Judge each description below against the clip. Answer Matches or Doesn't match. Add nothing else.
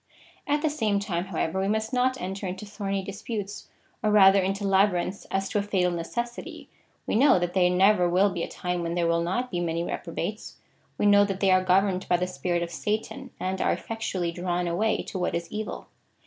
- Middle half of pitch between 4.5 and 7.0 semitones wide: Doesn't match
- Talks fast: Matches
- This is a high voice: Matches